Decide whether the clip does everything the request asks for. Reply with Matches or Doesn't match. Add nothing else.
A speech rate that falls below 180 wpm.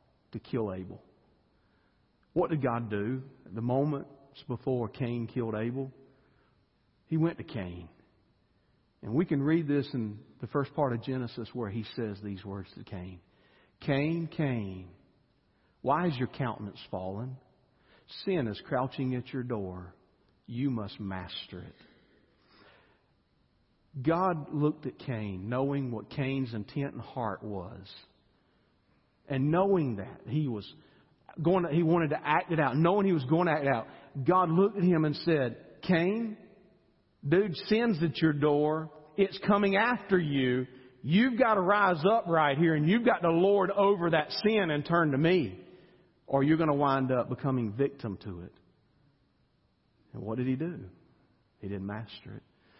Matches